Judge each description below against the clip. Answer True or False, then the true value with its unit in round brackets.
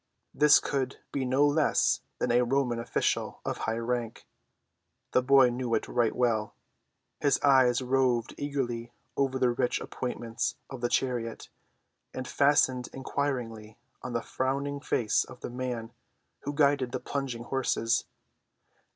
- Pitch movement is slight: True (2.3 semitones)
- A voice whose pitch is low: True (125 Hz)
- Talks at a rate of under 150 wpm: True (140 wpm)